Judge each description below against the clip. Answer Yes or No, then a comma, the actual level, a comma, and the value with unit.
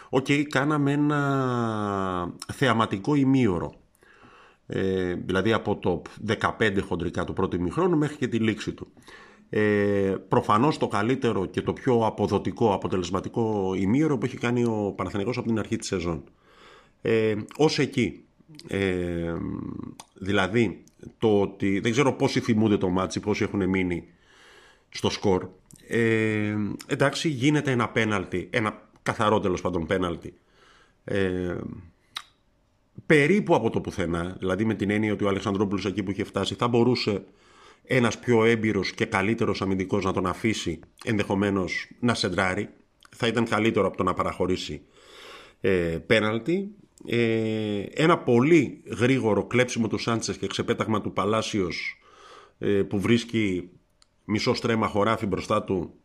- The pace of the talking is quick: No, average, 135 wpm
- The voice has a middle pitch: No, low, 105 Hz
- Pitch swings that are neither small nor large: Yes, average, 3.7 semitones